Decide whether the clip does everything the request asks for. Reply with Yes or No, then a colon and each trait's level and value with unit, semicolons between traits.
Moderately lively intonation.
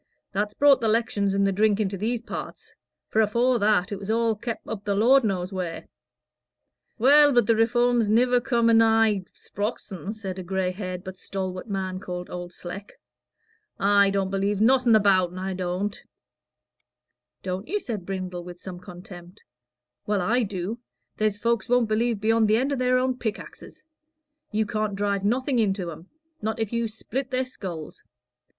Yes: average, 3.5 semitones